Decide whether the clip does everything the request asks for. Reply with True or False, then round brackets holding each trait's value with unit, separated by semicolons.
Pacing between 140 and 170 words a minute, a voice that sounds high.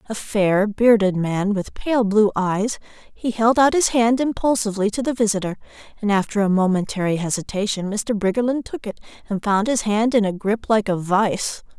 False (185 wpm; 210 Hz)